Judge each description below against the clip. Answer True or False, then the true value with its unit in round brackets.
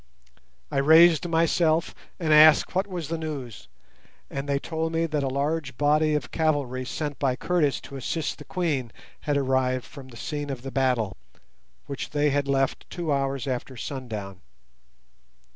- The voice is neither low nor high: True (145 Hz)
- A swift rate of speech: False (160 wpm)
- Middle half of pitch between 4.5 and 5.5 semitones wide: False (3.2 semitones)